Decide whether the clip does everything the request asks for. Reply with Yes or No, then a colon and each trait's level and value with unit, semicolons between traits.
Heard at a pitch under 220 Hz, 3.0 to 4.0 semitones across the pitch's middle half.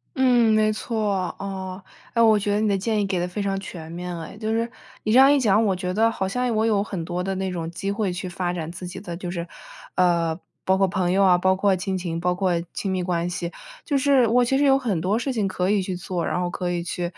Yes: high, 190 Hz; average, 3.4 semitones